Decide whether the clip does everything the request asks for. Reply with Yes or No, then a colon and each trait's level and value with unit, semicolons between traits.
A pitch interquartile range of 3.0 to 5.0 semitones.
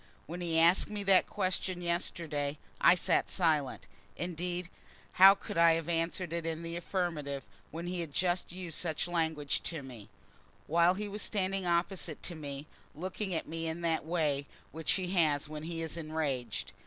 No: narrow, 2.5 semitones